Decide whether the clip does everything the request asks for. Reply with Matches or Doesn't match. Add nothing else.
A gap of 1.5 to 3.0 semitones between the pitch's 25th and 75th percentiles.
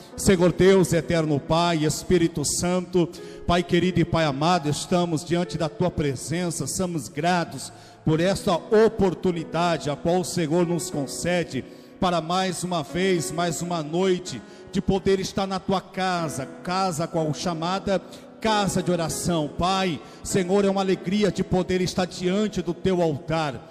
Matches